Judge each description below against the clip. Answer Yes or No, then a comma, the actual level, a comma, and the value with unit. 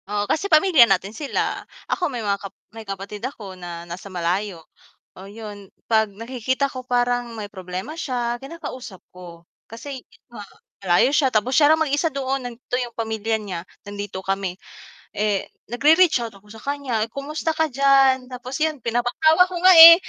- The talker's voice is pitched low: No, high, 235 Hz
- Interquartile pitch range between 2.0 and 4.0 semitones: No, wide, 5.4 semitones